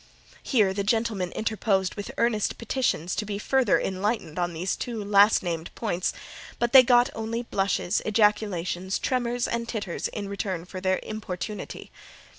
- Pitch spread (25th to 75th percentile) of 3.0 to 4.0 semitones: Yes, average, 3.6 semitones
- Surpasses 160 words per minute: No, average, 150 wpm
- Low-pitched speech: No, high, 205 Hz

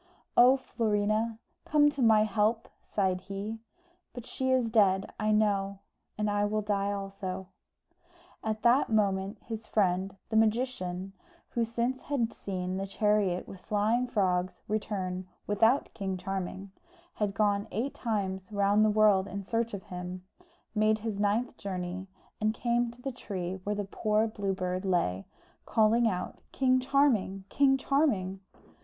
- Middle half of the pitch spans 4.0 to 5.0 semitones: No, average, 2.9 semitones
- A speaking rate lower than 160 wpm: Yes, average, 150 wpm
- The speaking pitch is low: No, high, 210 Hz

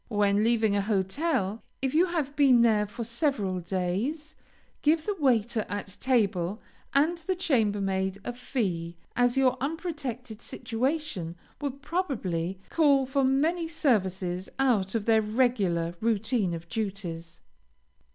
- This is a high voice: Yes, high, 230 Hz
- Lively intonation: Yes, wide, 6.1 semitones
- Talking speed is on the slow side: Yes, slow, 130 wpm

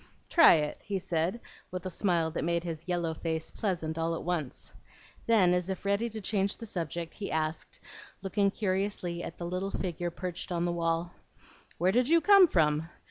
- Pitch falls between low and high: Yes, medium, 175 Hz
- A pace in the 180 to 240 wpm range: Yes, average, 190 wpm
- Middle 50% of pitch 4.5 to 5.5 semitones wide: No, average, 3.0 semitones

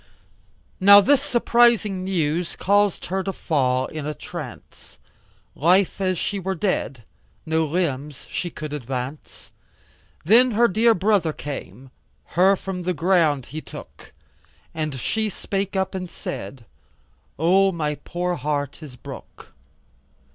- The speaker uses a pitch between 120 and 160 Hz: No, medium, 175 Hz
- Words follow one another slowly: Yes, slow, 125 wpm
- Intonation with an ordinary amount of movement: Yes, average, 4.7 semitones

